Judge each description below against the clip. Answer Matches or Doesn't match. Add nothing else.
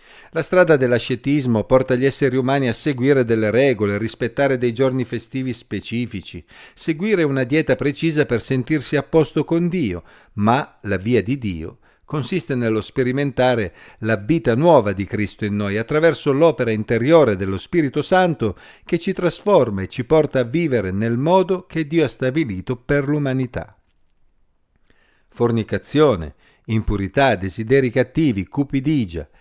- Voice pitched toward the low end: Matches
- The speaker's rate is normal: Matches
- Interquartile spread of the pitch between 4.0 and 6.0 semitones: Matches